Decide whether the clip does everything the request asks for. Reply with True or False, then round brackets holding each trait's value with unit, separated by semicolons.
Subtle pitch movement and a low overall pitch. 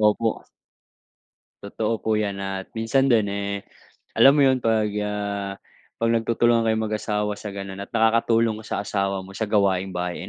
True (2.3 semitones; 105 Hz)